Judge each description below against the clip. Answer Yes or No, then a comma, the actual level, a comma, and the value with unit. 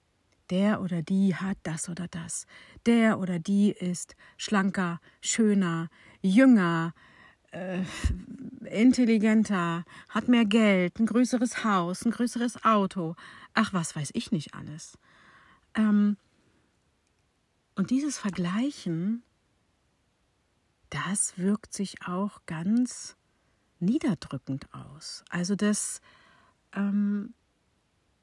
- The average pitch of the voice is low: No, high, 195 Hz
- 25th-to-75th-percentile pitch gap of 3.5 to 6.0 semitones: Yes, average, 4.7 semitones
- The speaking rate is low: Yes, slow, 95 wpm